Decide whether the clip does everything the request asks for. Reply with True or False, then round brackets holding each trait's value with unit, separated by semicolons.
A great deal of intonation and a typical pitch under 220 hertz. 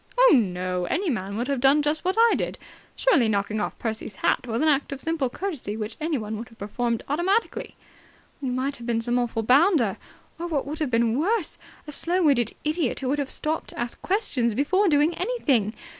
False (5.9 semitones; 270 Hz)